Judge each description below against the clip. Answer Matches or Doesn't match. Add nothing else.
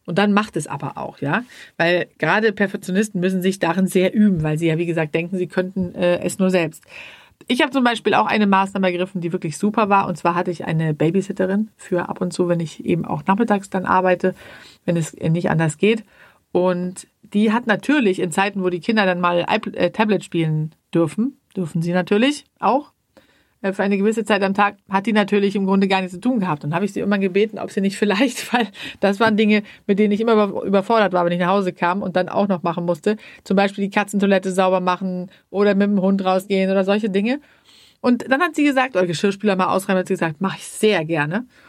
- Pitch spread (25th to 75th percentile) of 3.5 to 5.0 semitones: Doesn't match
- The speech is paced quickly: Matches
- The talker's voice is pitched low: Doesn't match